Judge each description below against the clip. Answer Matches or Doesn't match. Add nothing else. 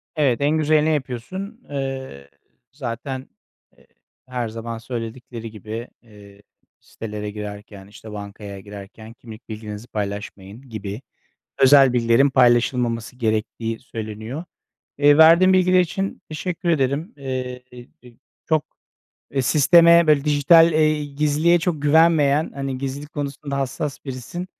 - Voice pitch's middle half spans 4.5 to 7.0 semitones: Matches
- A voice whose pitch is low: Matches